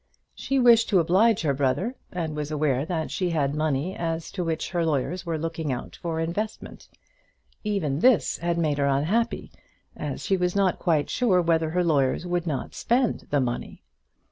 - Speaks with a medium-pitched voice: Yes, medium, 165 Hz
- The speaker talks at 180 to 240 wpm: Yes, average, 185 wpm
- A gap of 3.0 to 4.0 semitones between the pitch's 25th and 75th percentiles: Yes, average, 3.7 semitones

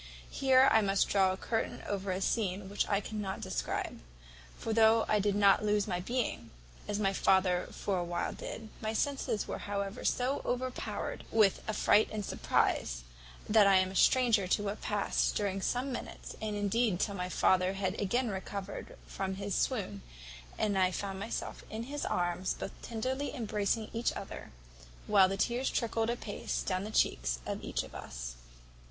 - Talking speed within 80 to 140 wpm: No, average, 175 wpm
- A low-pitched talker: No, high, 205 Hz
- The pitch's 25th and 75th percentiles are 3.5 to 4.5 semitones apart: No, average, 2.8 semitones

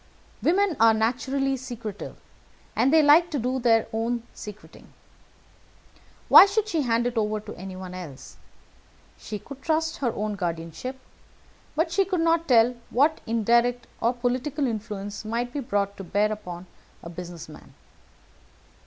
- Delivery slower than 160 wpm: Yes, average, 145 wpm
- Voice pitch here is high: Yes, high, 235 Hz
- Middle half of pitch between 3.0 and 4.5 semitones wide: No, average, 5.0 semitones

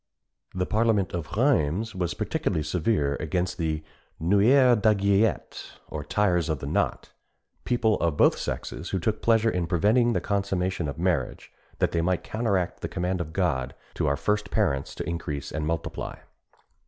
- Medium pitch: No, very low, 90 Hz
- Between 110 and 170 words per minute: Yes, average, 160 wpm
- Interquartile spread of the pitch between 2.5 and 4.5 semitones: No, average, 4.9 semitones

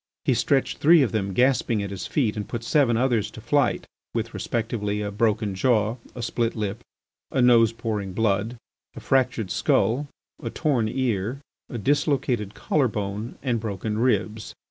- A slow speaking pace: No, average, 165 wpm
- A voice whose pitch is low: Yes, low, 115 Hz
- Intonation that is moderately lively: Yes, average, 3.2 semitones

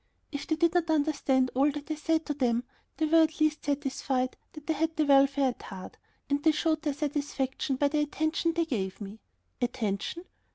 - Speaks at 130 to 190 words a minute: No, average, 200 wpm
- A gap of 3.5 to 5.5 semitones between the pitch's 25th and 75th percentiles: No, average, 3.0 semitones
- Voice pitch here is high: Yes, very high, 290 Hz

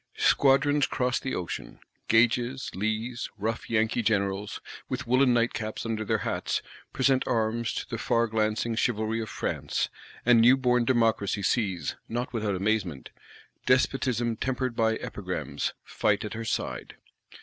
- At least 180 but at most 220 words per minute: No, average, 140 wpm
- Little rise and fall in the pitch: Yes, narrow, 2.2 semitones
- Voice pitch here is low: Yes, low, 115 Hz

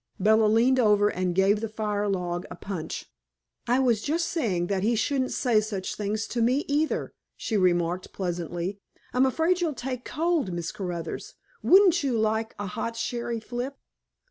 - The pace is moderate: Yes, average, 170 wpm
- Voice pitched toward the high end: Yes, high, 220 Hz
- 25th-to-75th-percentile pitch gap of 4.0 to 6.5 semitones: Yes, average, 5.0 semitones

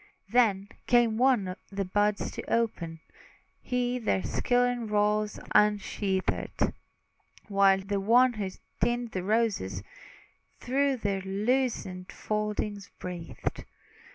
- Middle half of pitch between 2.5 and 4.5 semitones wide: Yes, average, 3.8 semitones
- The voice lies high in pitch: Yes, high, 210 Hz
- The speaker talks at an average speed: No, slow, 100 wpm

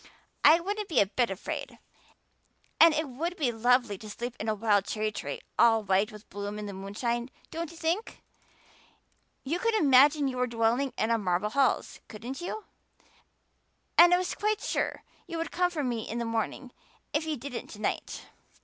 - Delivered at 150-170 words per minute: No, average, 185 wpm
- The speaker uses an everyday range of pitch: No, wide, 6.8 semitones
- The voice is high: Yes, high, 245 Hz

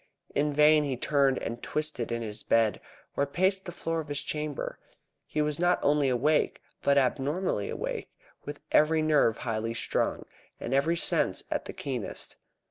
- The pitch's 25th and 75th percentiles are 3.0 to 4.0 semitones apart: Yes, average, 3.4 semitones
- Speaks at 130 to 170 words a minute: Yes, average, 165 wpm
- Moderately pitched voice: Yes, medium, 145 Hz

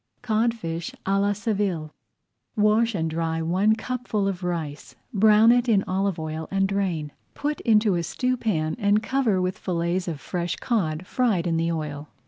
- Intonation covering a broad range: No, average, 4.6 semitones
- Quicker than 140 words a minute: Yes, average, 160 wpm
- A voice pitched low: No, high, 195 Hz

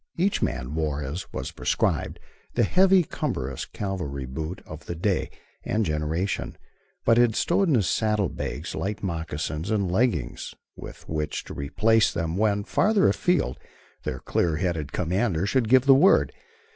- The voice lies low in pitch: Yes, very low, 95 Hz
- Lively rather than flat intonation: Yes, wide, 6.6 semitones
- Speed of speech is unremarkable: Yes, average, 155 wpm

